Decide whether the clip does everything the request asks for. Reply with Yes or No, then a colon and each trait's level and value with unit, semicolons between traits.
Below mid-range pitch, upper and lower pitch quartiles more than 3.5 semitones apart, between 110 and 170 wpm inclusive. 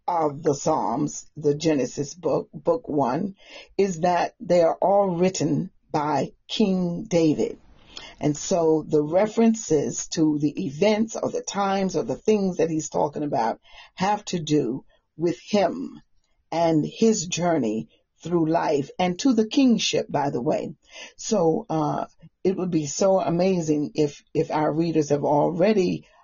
No: medium, 165 Hz; average, 4.3 semitones; average, 145 wpm